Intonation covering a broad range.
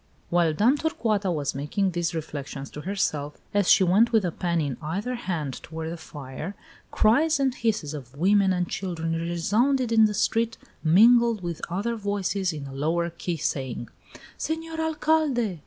Yes: wide, 6.0 semitones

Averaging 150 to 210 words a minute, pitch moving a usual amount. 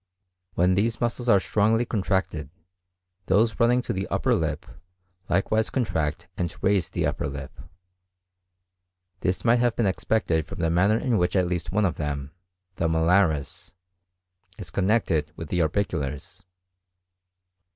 No: average, 140 wpm; average, 5.0 semitones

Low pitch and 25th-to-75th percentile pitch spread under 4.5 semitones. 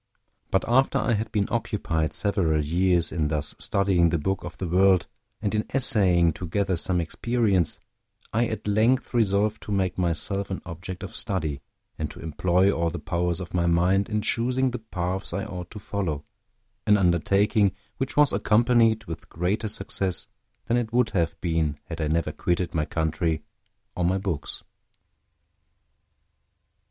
Yes: very low, 95 Hz; average, 3.9 semitones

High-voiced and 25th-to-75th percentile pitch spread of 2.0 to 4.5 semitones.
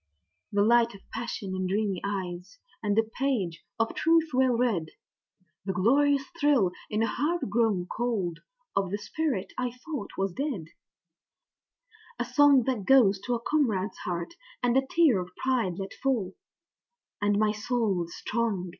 No: high, 220 Hz; average, 4.9 semitones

